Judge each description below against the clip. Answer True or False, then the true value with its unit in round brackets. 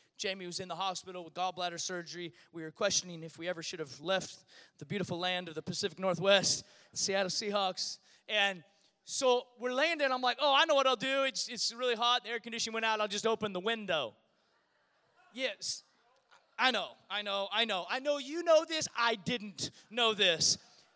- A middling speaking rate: True (195 wpm)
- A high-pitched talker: True (200 Hz)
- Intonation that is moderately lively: True (5.0 semitones)